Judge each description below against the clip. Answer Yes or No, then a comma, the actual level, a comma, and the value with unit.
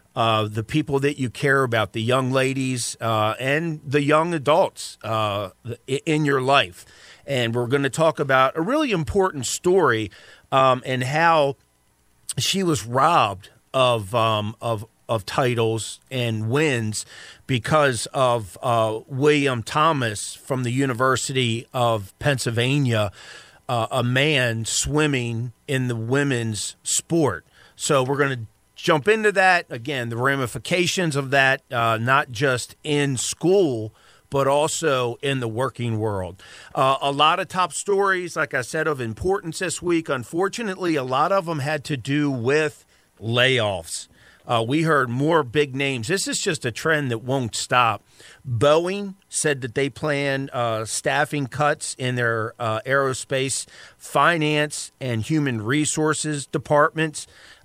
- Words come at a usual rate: Yes, average, 145 wpm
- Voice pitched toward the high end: No, low, 135 Hz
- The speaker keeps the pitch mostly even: No, average, 4.5 semitones